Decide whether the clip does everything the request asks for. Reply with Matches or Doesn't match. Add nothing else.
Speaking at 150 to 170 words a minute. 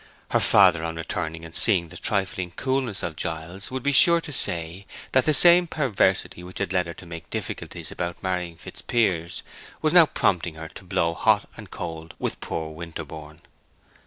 Doesn't match